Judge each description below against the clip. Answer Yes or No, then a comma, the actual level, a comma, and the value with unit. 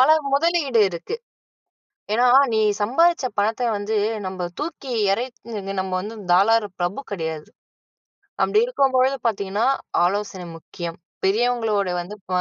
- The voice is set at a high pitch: Yes, high, 220 Hz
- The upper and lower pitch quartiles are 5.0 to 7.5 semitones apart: Yes, average, 5.3 semitones